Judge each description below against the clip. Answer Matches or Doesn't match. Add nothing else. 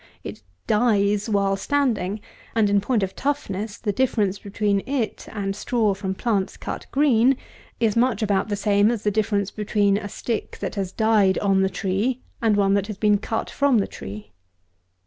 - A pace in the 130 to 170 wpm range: Doesn't match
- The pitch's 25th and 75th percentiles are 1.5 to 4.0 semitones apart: Matches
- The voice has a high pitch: Matches